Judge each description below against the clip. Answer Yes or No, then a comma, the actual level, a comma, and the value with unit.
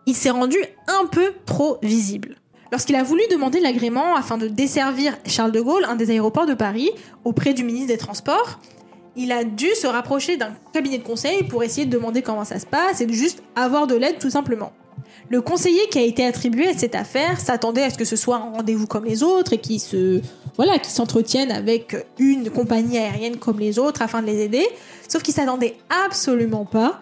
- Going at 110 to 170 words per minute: No, average, 210 wpm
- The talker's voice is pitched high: Yes, high, 245 Hz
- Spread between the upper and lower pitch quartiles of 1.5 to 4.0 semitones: No, average, 4.4 semitones